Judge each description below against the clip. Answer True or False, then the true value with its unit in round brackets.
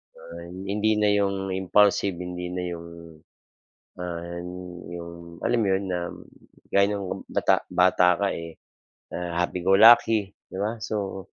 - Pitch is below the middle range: True (95 Hz)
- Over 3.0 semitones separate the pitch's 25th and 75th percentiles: False (2.6 semitones)